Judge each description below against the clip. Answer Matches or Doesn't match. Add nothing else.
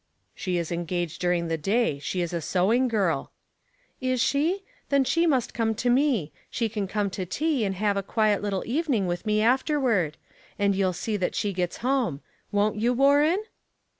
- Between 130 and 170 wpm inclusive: Doesn't match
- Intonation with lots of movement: Matches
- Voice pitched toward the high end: Matches